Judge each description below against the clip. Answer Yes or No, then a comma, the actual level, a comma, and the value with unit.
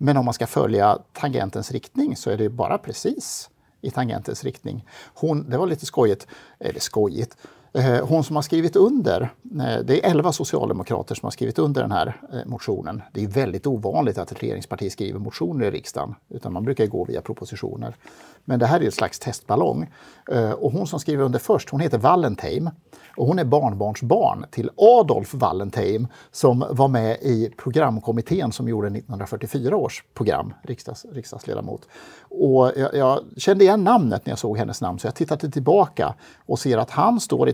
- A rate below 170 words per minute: No, average, 175 wpm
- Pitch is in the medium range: No, low, 130 Hz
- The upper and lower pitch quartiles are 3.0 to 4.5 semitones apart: No, average, 5.2 semitones